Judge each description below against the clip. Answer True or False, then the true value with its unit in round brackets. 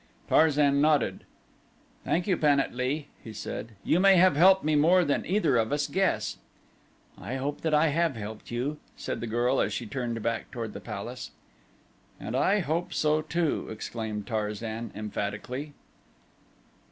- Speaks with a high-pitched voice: False (140 Hz)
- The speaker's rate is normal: True (160 wpm)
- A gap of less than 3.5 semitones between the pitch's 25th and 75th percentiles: False (5.4 semitones)